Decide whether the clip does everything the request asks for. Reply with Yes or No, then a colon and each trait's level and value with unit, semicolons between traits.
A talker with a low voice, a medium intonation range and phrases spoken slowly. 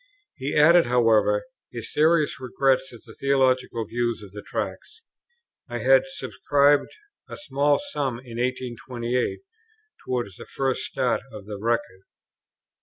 Yes: low, 130 Hz; average, 3.5 semitones; slow, 130 wpm